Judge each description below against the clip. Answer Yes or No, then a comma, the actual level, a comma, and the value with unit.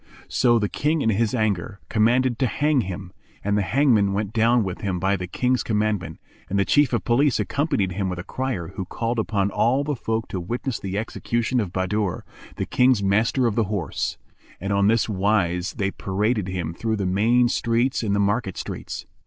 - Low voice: Yes, low, 105 Hz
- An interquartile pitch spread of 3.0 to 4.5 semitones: Yes, average, 3.7 semitones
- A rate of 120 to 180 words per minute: No, average, 200 wpm